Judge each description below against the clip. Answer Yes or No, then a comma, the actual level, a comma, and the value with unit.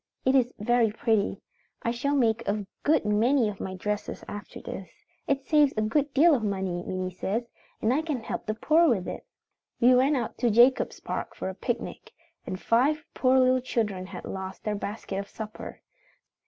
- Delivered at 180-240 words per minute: Yes, average, 190 wpm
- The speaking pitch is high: Yes, high, 230 Hz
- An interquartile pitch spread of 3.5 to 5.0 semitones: Yes, average, 4.3 semitones